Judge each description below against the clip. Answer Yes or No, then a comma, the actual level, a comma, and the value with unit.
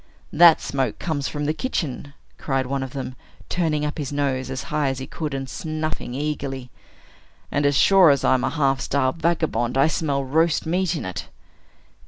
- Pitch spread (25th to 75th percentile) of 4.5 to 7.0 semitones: No, average, 2.9 semitones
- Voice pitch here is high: No, medium, 145 Hz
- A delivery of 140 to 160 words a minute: No, average, 185 wpm